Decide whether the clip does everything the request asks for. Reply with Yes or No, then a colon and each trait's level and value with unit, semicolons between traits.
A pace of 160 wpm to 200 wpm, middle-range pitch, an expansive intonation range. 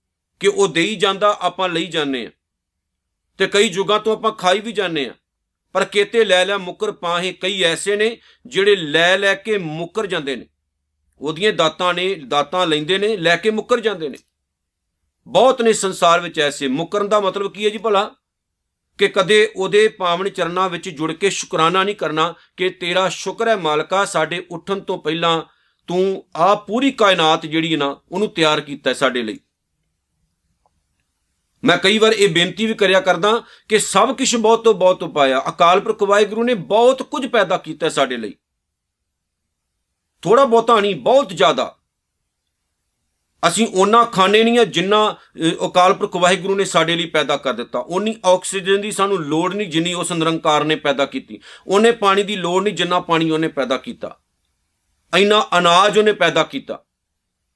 Yes: fast, 165 wpm; medium, 180 Hz; wide, 5.8 semitones